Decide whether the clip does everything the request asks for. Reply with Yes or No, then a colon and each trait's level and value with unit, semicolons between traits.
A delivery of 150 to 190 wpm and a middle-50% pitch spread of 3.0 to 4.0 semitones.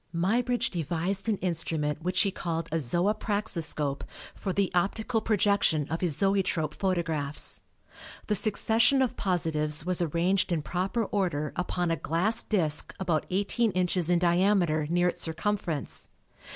No: average, 140 wpm; average, 3.7 semitones